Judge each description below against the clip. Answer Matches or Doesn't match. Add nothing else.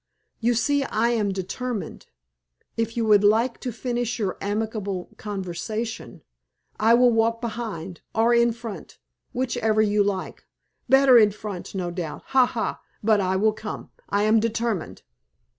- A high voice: Matches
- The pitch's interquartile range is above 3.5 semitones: Doesn't match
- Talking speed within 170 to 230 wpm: Doesn't match